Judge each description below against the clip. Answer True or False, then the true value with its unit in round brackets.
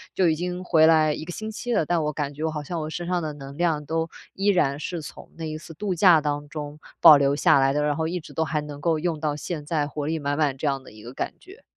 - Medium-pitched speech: True (155 Hz)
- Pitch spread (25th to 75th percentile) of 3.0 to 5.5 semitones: False (2.5 semitones)